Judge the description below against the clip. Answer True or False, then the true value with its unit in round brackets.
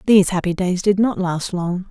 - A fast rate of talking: True (220 wpm)